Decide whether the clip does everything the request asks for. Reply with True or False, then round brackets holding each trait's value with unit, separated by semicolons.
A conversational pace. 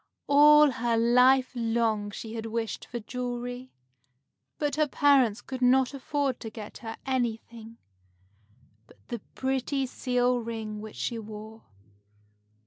False (130 wpm)